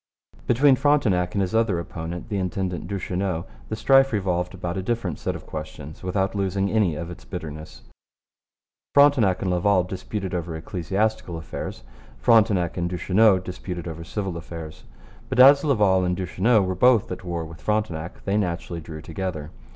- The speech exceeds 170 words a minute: No, average, 160 wpm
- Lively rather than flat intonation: No, average, 3.5 semitones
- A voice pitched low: Yes, very low, 95 Hz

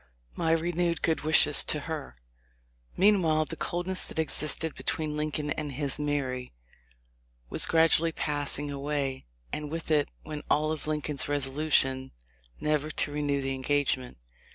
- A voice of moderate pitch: Yes, medium, 150 Hz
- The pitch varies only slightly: Yes, narrow, 1.9 semitones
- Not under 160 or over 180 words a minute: No, slow, 135 wpm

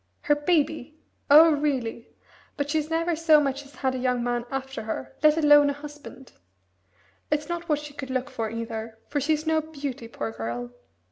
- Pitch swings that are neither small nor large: Yes, average, 3.5 semitones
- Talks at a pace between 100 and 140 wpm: No, average, 185 wpm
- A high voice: Yes, very high, 285 Hz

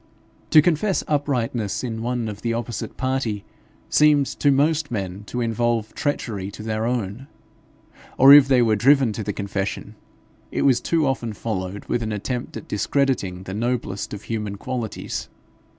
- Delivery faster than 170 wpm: No, average, 160 wpm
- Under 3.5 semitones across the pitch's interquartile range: No, average, 4.3 semitones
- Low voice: Yes, low, 115 Hz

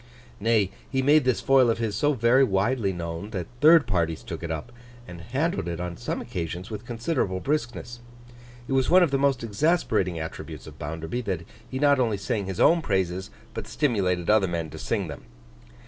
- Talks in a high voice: No, low, 110 Hz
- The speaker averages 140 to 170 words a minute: No, average, 195 wpm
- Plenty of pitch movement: Yes, wide, 6.7 semitones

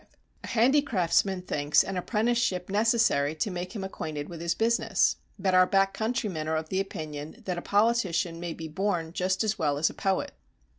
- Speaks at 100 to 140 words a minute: No, average, 180 wpm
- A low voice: No, medium, 185 Hz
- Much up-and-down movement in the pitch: No, average, 4.6 semitones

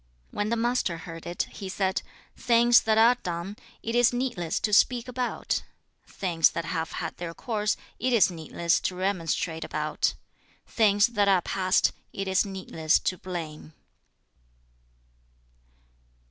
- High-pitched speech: Yes, high, 195 Hz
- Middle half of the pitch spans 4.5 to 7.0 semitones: Yes, average, 5.0 semitones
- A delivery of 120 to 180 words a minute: Yes, average, 145 wpm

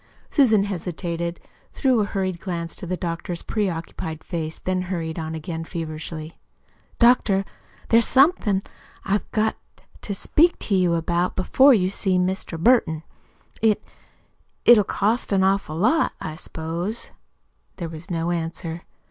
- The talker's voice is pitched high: No, medium, 180 Hz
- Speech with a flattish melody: No, average, 3.8 semitones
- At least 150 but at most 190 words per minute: No, average, 140 wpm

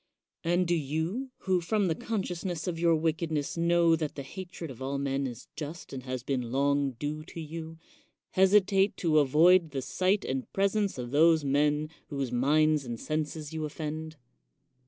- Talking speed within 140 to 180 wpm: Yes, average, 170 wpm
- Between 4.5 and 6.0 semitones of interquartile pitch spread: No, average, 3.6 semitones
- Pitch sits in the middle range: Yes, medium, 155 Hz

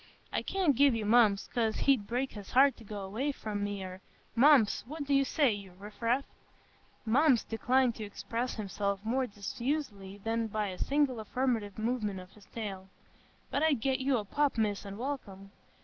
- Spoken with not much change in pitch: No, average, 4.7 semitones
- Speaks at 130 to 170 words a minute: No, average, 180 wpm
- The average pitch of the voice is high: Yes, high, 225 Hz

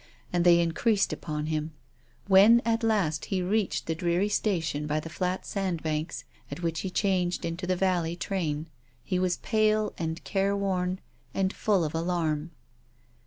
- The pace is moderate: Yes, average, 155 wpm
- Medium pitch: Yes, medium, 180 Hz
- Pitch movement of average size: Yes, average, 3.2 semitones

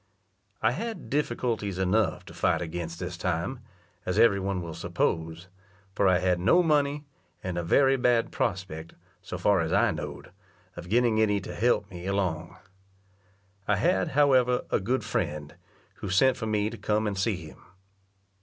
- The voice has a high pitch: No, low, 100 Hz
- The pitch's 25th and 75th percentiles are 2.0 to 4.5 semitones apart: No, average, 5.2 semitones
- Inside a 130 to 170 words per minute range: Yes, average, 165 wpm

